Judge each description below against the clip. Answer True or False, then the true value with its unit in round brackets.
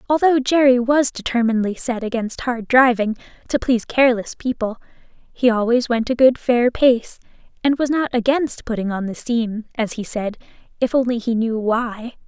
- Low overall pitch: False (240 Hz)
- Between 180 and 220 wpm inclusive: False (170 wpm)